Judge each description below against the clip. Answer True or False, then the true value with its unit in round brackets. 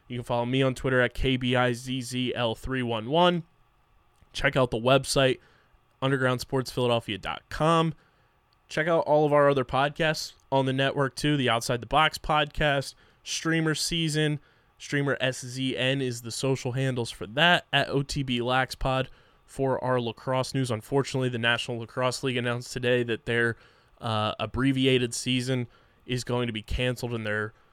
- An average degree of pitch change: False (2.3 semitones)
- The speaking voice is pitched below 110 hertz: False (130 Hz)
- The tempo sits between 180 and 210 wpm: False (145 wpm)